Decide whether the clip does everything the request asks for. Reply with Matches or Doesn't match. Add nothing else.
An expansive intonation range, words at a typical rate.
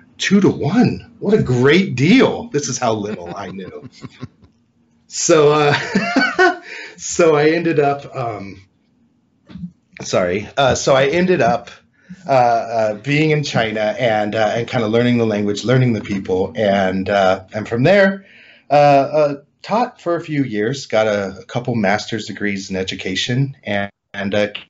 Matches